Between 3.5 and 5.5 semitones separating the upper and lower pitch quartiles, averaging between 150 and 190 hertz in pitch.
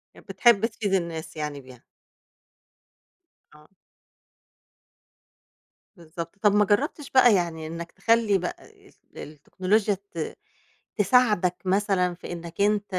Yes: average, 3.8 semitones; medium, 185 Hz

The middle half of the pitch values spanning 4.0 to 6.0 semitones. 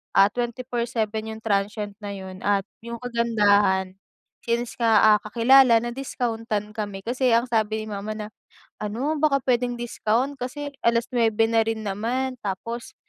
No: narrow, 2.6 semitones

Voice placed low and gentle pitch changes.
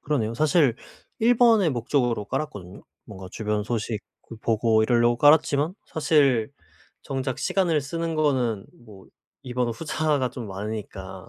No: low, 125 Hz; wide, 5.6 semitones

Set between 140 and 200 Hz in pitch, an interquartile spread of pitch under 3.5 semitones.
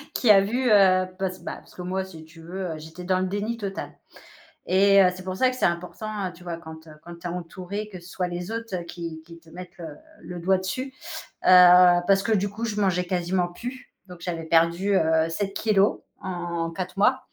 Yes: medium, 185 Hz; narrow, 2.4 semitones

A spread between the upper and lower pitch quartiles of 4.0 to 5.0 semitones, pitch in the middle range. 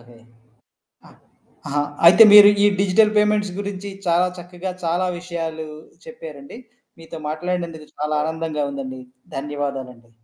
Yes: average, 4.4 semitones; medium, 170 Hz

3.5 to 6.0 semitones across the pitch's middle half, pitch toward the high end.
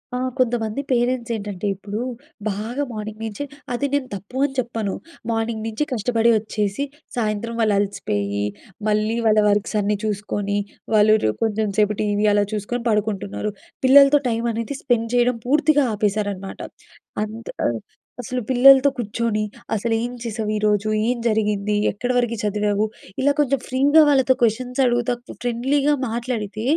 No: average, 2.9 semitones; high, 220 Hz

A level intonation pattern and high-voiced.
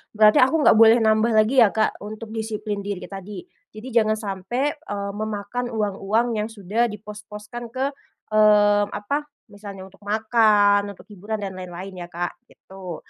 Yes: narrow, 1.7 semitones; high, 210 Hz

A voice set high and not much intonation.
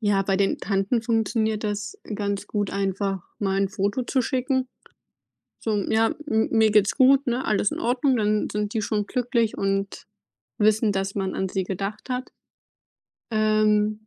Yes: high, 210 Hz; narrow, 2.3 semitones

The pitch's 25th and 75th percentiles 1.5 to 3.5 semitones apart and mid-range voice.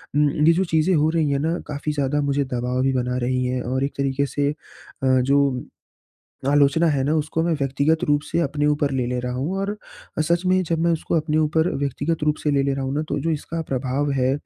Yes: average, 2.8 semitones; medium, 145 Hz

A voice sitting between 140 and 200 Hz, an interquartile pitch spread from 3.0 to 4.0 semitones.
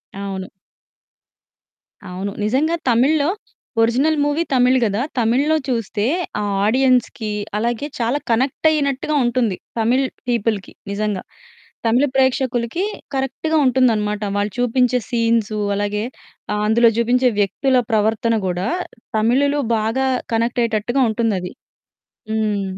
No: high, 235 Hz; average, 3.6 semitones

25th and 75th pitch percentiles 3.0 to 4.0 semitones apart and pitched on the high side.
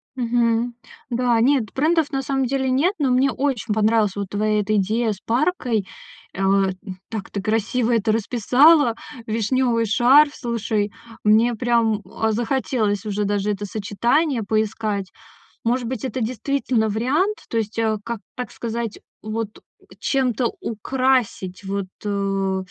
Yes: average, 3.3 semitones; high, 230 Hz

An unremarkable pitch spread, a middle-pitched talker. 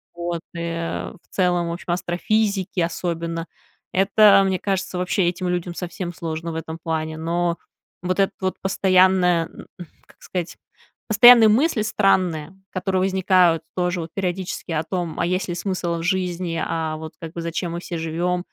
No: narrow, 2.0 semitones; medium, 175 Hz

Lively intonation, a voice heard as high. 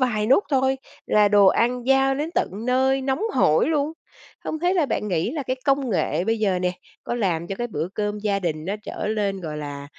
Yes: wide, 6.2 semitones; high, 215 Hz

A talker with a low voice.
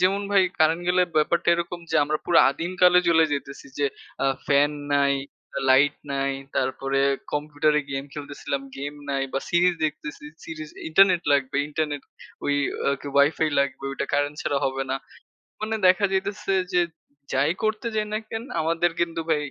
No: medium, 155 Hz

